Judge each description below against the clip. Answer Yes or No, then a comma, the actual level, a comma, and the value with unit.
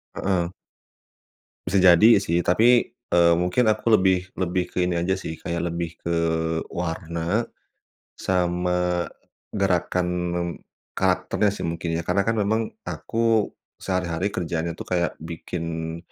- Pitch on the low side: Yes, very low, 90 Hz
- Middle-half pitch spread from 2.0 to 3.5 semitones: Yes, narrow, 2.4 semitones